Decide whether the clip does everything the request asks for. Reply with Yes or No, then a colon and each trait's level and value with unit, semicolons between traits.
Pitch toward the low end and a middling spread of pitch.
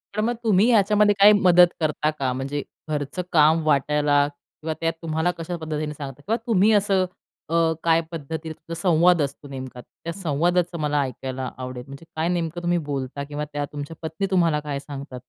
No: medium, 155 Hz; average, 3.6 semitones